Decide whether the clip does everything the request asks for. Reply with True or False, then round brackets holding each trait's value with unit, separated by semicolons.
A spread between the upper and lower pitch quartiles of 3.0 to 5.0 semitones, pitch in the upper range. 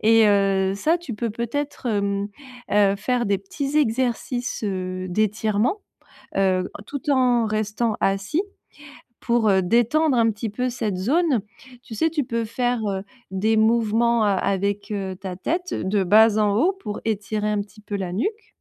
True (3.4 semitones; 215 Hz)